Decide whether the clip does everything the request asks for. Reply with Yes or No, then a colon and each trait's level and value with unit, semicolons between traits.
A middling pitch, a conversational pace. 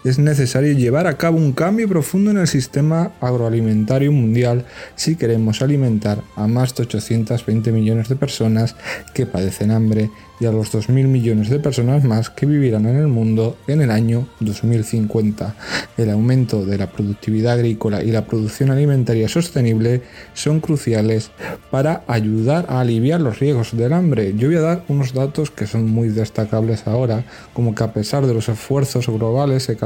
No: low, 120 Hz; average, 170 wpm